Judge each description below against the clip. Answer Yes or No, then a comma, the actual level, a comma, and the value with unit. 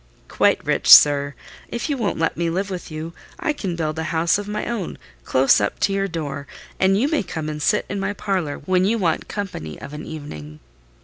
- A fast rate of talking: Yes, fast, 215 wpm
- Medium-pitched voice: Yes, medium, 170 Hz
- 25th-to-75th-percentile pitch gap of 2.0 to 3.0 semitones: No, average, 4.8 semitones